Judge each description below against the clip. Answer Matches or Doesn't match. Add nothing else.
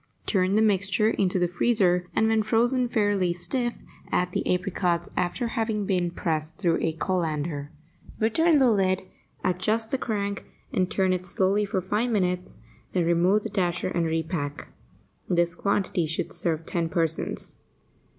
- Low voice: Doesn't match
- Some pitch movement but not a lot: Matches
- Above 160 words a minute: Doesn't match